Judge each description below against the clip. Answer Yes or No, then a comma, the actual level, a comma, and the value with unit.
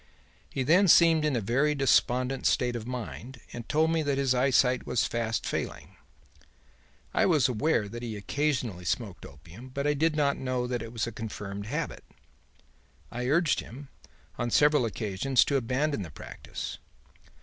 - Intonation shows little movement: No, average, 4.0 semitones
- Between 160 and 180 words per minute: Yes, average, 165 wpm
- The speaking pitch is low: Yes, low, 125 Hz